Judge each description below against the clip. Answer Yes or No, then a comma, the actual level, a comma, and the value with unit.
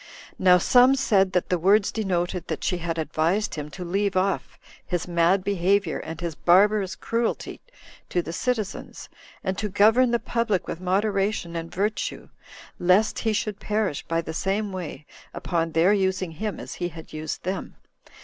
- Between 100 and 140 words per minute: No, average, 170 wpm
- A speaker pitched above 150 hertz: Yes, medium, 185 Hz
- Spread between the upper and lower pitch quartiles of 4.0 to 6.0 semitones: No, average, 3.4 semitones